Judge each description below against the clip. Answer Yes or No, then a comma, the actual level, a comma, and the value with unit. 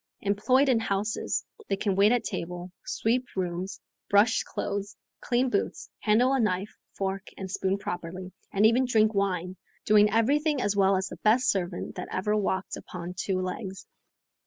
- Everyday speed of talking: Yes, average, 160 wpm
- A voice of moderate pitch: No, high, 200 Hz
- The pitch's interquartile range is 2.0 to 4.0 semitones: Yes, average, 3.1 semitones